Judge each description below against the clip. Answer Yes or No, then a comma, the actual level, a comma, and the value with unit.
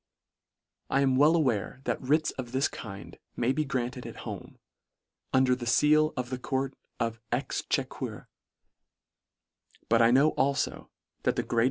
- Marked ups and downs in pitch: No, narrow, 2.6 semitones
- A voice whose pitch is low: Yes, low, 130 Hz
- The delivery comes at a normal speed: Yes, average, 150 wpm